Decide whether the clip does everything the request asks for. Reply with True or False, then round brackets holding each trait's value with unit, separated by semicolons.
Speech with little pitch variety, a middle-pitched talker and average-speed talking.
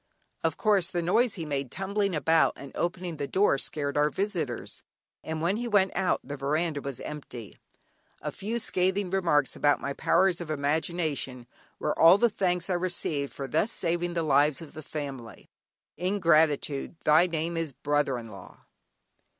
False (4.2 semitones; 160 Hz; 165 wpm)